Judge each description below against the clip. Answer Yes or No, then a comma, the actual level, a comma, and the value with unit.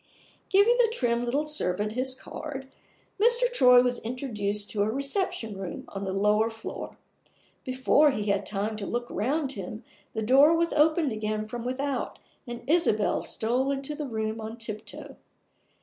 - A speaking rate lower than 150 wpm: No, average, 160 wpm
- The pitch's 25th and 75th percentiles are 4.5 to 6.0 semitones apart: Yes, average, 4.8 semitones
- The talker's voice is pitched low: No, high, 245 Hz